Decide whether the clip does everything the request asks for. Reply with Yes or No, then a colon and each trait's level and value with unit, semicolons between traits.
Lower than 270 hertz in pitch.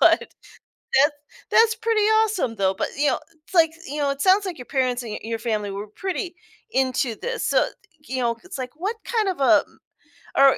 No: very high, 280 Hz